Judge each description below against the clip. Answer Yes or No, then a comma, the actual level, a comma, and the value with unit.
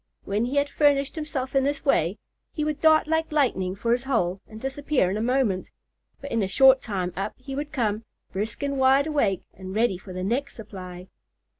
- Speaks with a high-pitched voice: Yes, very high, 250 Hz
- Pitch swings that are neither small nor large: No, wide, 6.3 semitones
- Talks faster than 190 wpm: Yes, fast, 205 wpm